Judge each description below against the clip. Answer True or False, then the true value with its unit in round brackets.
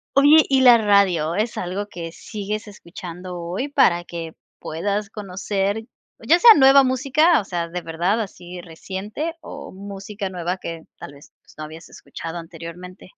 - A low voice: False (195 Hz)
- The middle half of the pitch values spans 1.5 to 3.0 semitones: False (4.4 semitones)